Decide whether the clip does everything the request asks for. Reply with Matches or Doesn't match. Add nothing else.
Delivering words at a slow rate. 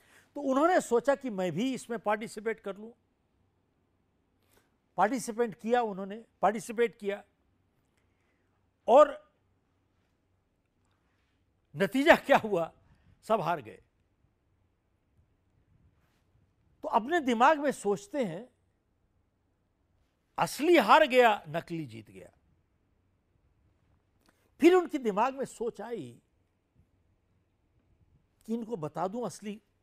Matches